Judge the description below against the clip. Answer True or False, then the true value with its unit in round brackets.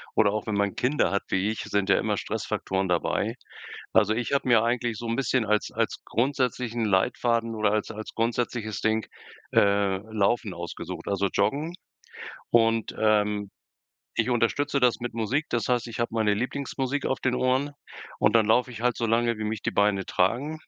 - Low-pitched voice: True (115 Hz)